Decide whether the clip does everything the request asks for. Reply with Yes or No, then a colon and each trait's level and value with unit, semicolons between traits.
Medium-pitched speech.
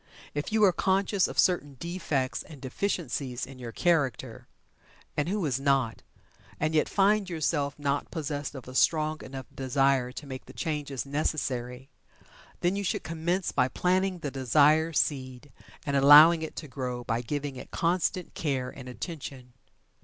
Yes: medium, 145 Hz